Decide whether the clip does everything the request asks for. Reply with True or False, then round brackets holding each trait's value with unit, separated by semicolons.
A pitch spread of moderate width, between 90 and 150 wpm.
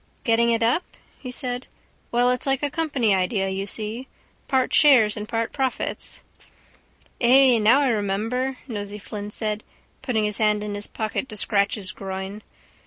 False (3.3 semitones; 165 wpm)